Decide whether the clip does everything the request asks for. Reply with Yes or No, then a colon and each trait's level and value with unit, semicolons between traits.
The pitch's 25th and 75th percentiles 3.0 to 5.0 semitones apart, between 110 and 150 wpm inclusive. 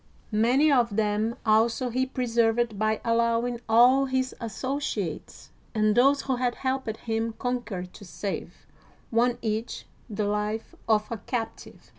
No: narrow, 2.5 semitones; average, 140 wpm